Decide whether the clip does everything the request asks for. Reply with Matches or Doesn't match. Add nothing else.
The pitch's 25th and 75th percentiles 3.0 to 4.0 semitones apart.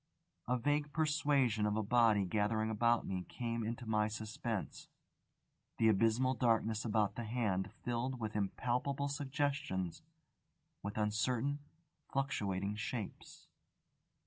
Matches